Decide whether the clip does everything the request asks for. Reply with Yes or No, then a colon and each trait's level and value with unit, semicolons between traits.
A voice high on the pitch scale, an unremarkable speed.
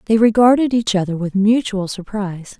Yes: high, 210 Hz; average, 160 wpm